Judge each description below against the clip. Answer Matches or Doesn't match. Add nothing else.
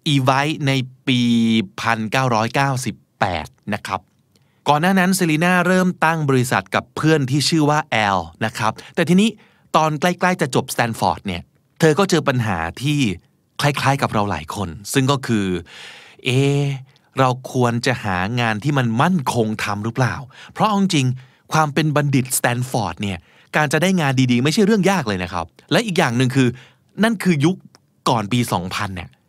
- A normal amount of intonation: Doesn't match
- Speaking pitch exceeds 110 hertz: Matches